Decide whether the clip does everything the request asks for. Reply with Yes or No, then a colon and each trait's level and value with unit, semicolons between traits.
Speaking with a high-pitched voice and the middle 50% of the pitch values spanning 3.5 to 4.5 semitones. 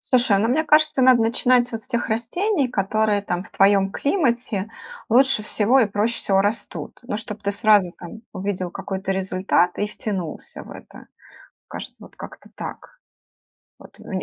Yes: high, 215 Hz; average, 3.9 semitones